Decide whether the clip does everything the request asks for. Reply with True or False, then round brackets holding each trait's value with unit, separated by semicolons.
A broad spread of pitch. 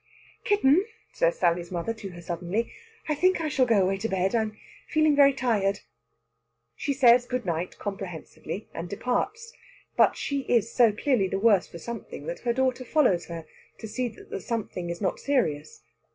True (5.9 semitones)